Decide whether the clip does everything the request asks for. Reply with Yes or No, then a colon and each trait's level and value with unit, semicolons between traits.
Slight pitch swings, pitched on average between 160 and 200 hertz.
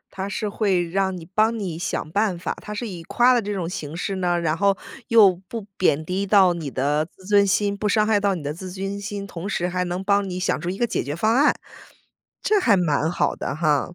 No: average, 3.0 semitones; high, 190 Hz